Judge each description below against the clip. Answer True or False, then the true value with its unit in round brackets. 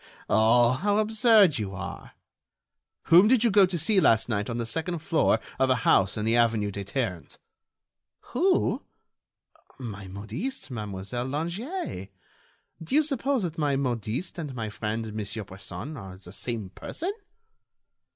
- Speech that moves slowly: False (150 wpm)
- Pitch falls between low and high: False (125 Hz)